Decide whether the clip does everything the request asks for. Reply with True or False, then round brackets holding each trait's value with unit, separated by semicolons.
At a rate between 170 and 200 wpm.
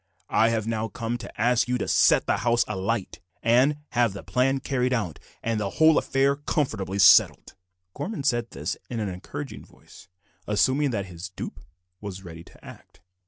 True (175 wpm)